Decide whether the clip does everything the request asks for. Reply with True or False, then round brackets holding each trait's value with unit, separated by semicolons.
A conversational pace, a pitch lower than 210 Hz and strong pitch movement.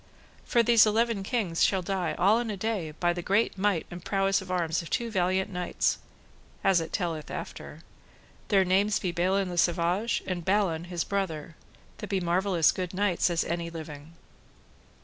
False (180 wpm; 185 Hz; 2.7 semitones)